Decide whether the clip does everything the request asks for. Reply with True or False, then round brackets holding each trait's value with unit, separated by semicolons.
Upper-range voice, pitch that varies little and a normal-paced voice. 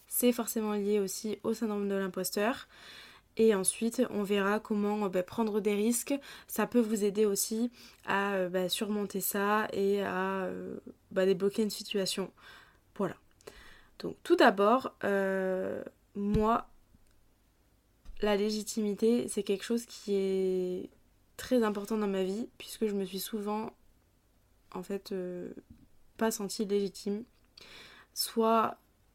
False (205 Hz; 2.3 semitones; 135 wpm)